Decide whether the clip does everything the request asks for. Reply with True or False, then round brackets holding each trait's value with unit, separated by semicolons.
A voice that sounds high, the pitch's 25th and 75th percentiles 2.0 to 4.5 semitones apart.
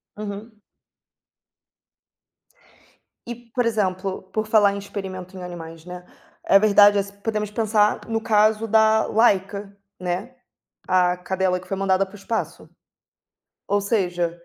True (200 Hz; 2.7 semitones)